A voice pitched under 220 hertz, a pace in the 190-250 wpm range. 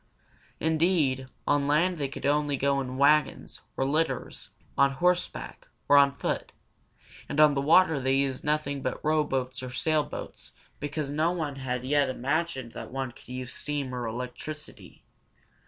No: medium, 140 Hz; average, 155 wpm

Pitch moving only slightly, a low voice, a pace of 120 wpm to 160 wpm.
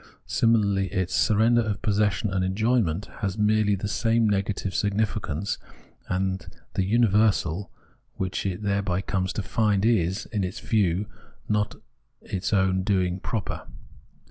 Yes: narrow, 2.3 semitones; low, 100 Hz; slow, 135 wpm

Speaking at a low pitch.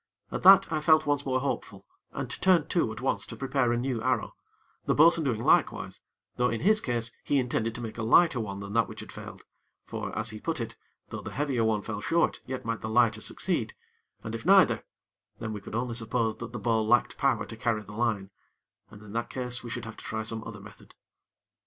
Yes: low, 115 Hz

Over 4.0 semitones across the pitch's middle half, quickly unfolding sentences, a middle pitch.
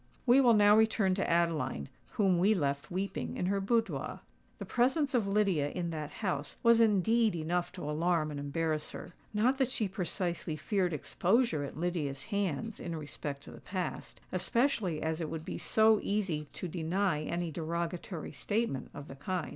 No: average, 5.1 semitones; average, 170 wpm; medium, 180 Hz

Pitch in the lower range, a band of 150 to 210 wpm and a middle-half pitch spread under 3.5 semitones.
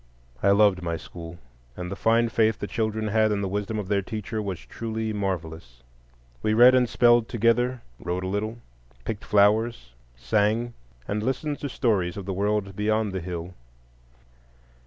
Yes: low, 105 Hz; average, 165 wpm; average, 3.1 semitones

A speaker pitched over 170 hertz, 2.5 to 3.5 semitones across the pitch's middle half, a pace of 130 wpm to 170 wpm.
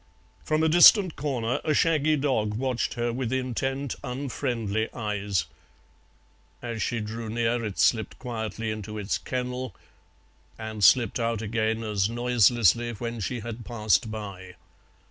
No: low, 115 Hz; average, 2.8 semitones; slow, 135 wpm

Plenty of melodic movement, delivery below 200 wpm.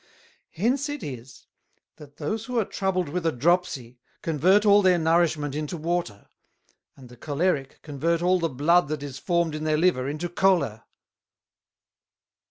No: average, 4.0 semitones; average, 155 wpm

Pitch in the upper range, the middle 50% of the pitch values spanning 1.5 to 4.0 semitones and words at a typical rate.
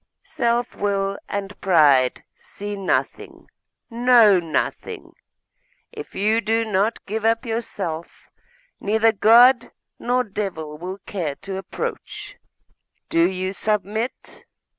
No: high, 205 Hz; average, 3.3 semitones; slow, 105 wpm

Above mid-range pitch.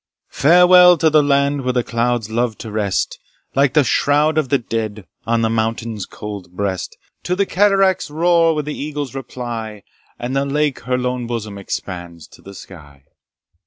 No: low, 125 Hz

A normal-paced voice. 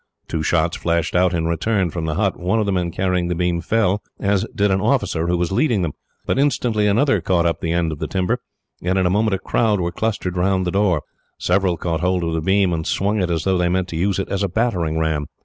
No: fast, 255 wpm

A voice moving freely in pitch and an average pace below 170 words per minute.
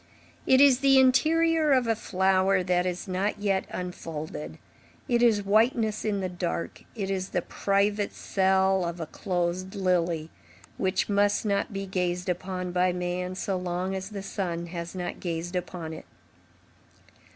No: narrow, 2.4 semitones; average, 155 wpm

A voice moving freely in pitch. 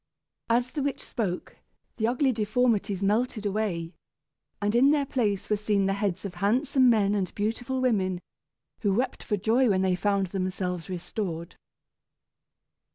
No: average, 4.1 semitones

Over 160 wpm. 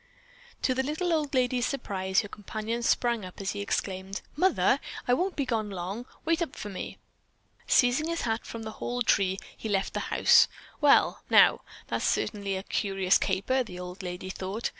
Yes: average, 185 wpm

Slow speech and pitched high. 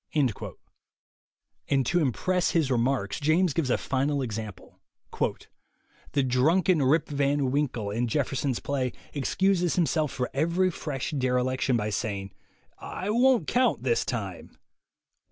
No: slow, 130 wpm; medium, 140 Hz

